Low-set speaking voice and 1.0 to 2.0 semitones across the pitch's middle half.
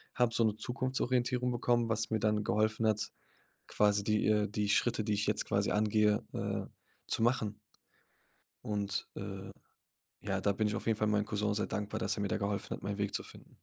Yes: low, 105 Hz; narrow, 1.6 semitones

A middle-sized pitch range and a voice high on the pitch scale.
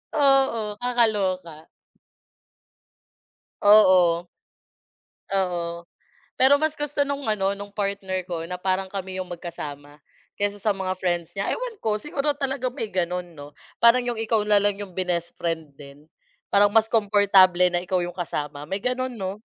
Yes: average, 4.2 semitones; high, 195 Hz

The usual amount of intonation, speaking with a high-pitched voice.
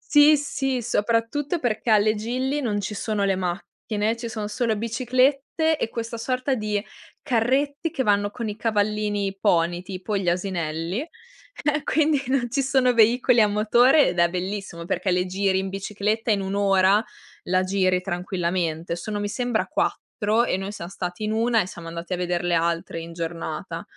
Yes: average, 4.8 semitones; high, 210 Hz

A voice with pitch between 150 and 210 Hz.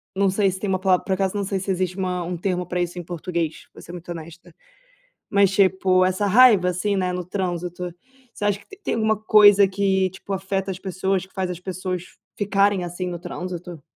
Yes: medium, 185 Hz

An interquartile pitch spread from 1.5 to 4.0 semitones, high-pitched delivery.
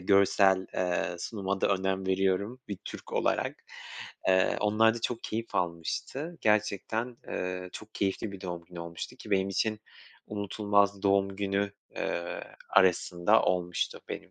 No: narrow, 2.4 semitones; low, 100 Hz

